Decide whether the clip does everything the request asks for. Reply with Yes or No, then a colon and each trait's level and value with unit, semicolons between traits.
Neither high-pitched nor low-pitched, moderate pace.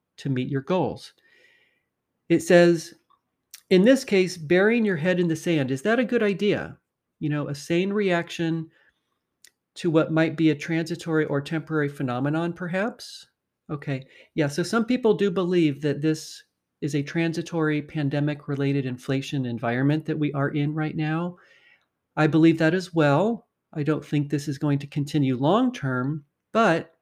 Yes: medium, 160 Hz; average, 160 wpm